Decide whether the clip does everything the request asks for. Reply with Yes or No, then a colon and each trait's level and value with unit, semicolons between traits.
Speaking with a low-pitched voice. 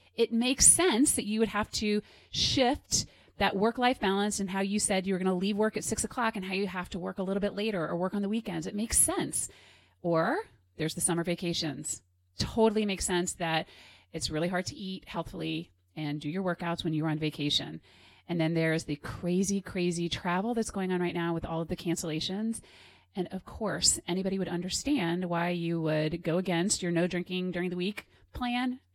No: medium, 180 Hz